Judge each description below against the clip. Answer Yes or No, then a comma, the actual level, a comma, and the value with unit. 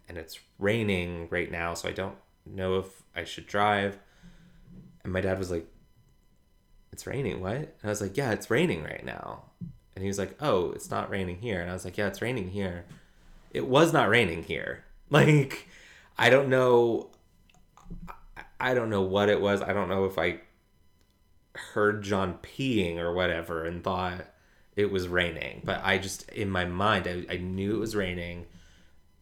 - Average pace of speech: Yes, average, 185 wpm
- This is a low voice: Yes, very low, 95 Hz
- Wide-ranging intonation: No, average, 2.7 semitones